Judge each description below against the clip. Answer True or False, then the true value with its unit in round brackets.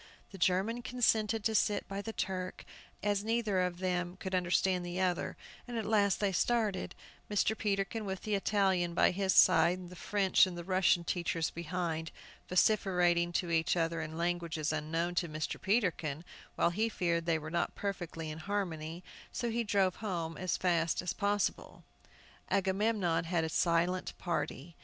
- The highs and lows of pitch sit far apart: False (3.0 semitones)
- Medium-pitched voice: True (180 Hz)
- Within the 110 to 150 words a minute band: False (165 wpm)